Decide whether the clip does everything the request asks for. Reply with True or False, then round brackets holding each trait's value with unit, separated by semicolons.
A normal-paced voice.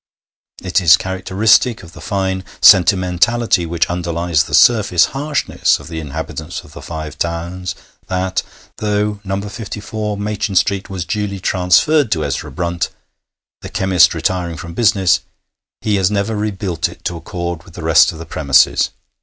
True (155 wpm)